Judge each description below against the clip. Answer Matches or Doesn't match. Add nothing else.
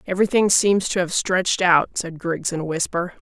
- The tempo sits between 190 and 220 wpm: Matches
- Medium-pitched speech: Matches